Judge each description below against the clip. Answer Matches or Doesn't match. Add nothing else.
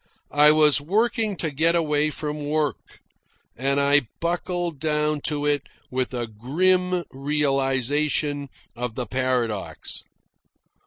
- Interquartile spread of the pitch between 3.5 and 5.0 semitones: Doesn't match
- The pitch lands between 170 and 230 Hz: Doesn't match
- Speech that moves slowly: Matches